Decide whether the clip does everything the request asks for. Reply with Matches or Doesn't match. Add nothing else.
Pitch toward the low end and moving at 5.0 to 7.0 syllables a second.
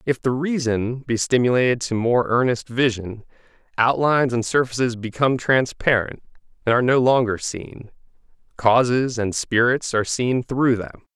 Doesn't match